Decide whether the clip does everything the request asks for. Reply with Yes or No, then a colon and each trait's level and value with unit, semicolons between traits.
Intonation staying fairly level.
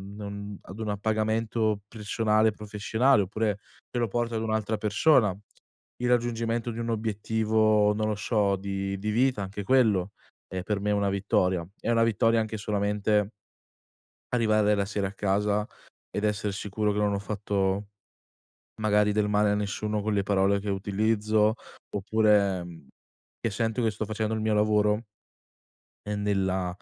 Yes: narrow, 1.5 semitones